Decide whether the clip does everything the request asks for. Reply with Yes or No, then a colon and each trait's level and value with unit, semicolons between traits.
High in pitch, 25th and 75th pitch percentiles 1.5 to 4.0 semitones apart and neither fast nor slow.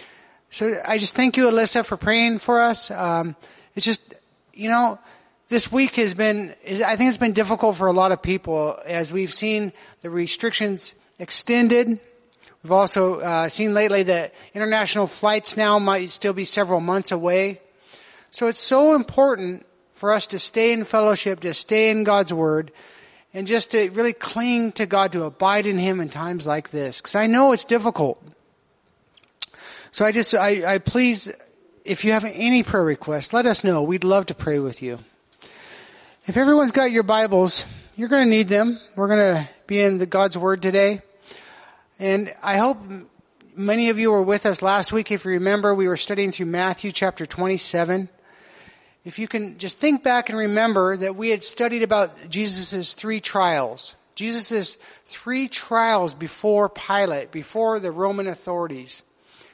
Yes: high, 205 Hz; average, 3.4 semitones; average, 170 wpm